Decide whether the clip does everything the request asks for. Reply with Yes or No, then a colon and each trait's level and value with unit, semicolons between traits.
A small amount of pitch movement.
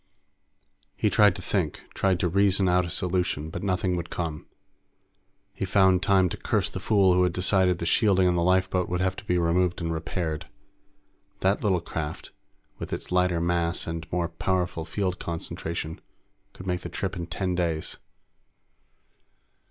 Yes: narrow, 1.8 semitones